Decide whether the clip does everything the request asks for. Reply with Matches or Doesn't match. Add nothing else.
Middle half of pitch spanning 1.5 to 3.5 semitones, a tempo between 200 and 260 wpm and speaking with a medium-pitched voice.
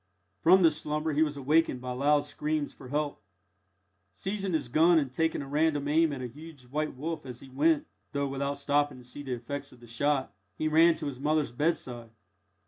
Matches